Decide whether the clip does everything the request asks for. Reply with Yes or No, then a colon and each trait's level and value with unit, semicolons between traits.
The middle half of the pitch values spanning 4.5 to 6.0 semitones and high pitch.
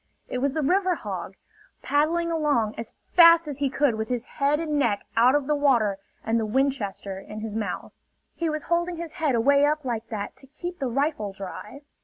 Yes: wide, 5.4 semitones; very high, 275 Hz